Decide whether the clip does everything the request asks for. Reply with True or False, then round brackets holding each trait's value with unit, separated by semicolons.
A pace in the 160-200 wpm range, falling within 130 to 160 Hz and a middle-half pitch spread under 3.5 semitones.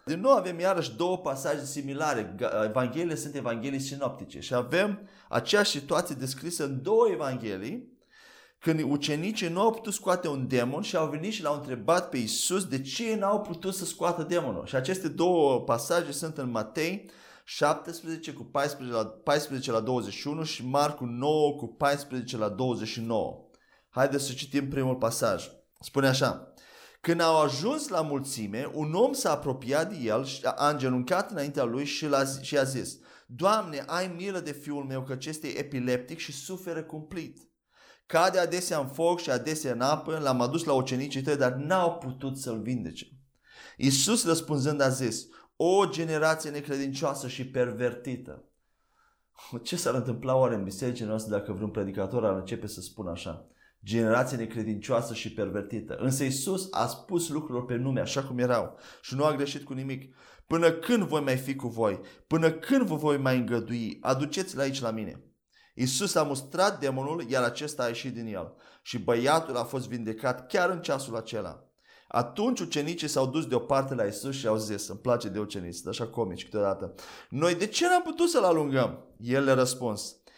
False (170 wpm; 140 Hz; 4.7 semitones)